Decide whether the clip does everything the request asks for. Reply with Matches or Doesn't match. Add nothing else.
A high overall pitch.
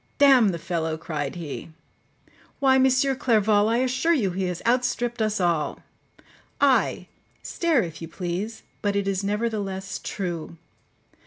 Matches